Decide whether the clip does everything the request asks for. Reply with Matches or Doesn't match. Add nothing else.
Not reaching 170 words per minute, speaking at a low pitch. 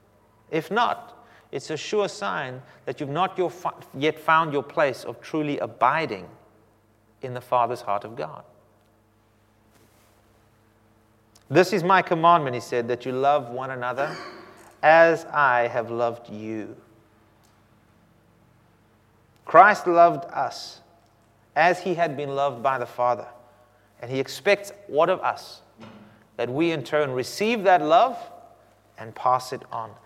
Matches